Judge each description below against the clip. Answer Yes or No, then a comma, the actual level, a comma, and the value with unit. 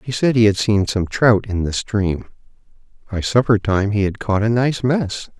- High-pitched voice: No, low, 110 Hz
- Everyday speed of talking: No, fast, 210 wpm